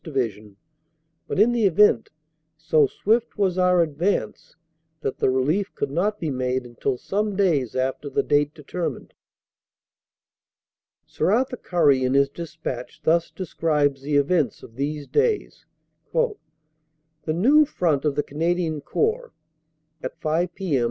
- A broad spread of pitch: Yes, wide, 5.8 semitones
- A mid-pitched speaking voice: Yes, medium, 160 Hz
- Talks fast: No, slow, 135 wpm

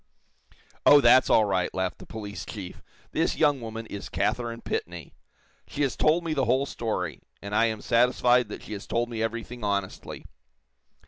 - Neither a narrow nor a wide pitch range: Yes, average, 3.4 semitones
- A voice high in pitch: No, low, 115 Hz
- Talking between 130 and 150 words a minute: No, average, 175 wpm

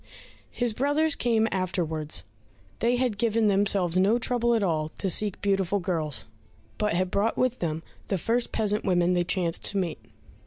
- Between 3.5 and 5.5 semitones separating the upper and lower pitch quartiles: Yes, average, 4.5 semitones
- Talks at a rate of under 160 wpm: No, average, 165 wpm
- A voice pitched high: Yes, high, 200 Hz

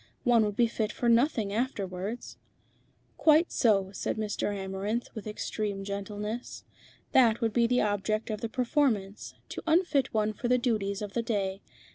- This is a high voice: Yes, high, 215 Hz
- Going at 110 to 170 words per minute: Yes, average, 160 wpm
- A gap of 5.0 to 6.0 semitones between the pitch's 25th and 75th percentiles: No, average, 3.0 semitones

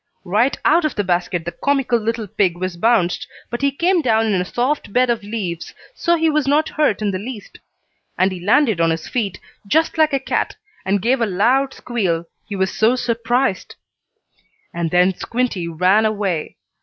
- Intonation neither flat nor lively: No, wide, 5.8 semitones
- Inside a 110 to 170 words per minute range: No, average, 185 wpm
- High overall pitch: Yes, high, 220 Hz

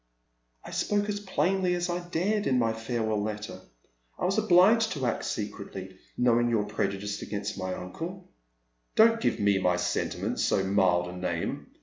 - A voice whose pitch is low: Yes, low, 115 Hz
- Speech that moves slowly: No, average, 165 wpm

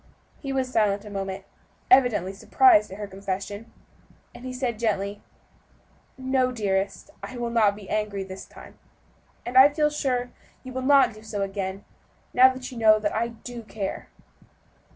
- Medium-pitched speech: No, high, 220 Hz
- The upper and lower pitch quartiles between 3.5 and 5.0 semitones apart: Yes, average, 4.2 semitones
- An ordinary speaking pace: Yes, average, 160 wpm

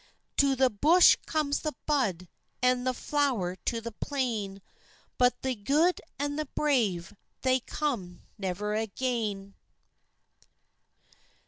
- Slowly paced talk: Yes, slow, 115 wpm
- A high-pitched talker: Yes, very high, 250 Hz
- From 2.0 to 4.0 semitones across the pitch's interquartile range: No, wide, 5.6 semitones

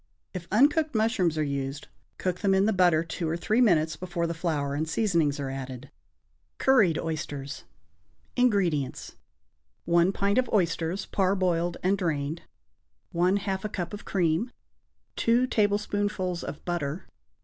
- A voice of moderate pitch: Yes, medium, 175 Hz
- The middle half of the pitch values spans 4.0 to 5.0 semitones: Yes, average, 4.3 semitones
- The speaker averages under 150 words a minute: Yes, average, 140 wpm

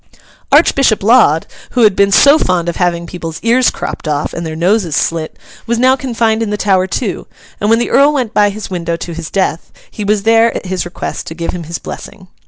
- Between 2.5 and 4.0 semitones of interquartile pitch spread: No, average, 5.1 semitones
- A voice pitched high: Yes, high, 195 Hz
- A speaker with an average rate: No, fast, 220 wpm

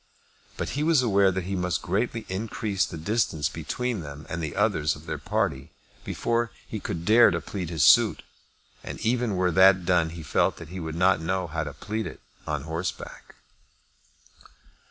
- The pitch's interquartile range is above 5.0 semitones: No, average, 4.7 semitones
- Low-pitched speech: Yes, very low, 90 Hz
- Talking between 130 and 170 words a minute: No, average, 180 wpm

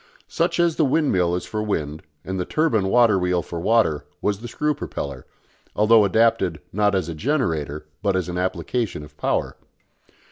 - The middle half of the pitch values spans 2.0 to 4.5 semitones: No, average, 5.2 semitones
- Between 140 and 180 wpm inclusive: Yes, average, 175 wpm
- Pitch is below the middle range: Yes, very low, 95 Hz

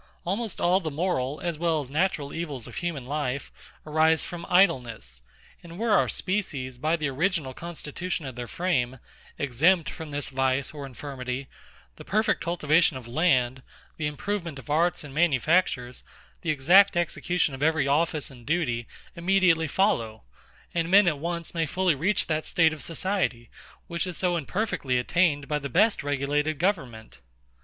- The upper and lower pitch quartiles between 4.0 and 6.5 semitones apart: Yes, average, 4.3 semitones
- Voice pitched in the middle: Yes, medium, 155 Hz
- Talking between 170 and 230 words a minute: No, average, 160 wpm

